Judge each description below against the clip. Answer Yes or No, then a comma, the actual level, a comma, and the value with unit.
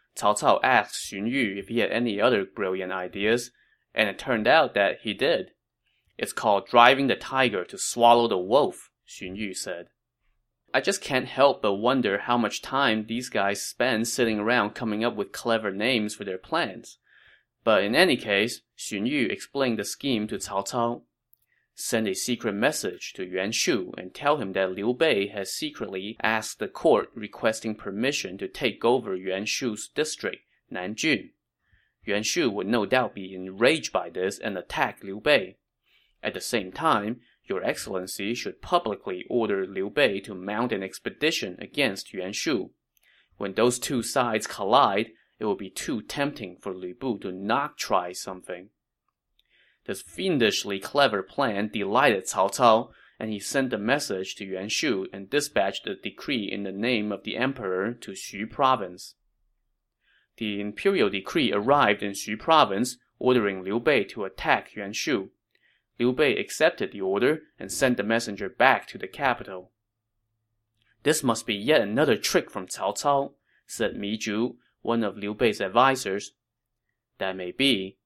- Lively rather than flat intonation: No, average, 3.6 semitones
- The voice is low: Yes, low, 110 Hz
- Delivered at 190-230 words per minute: No, average, 165 wpm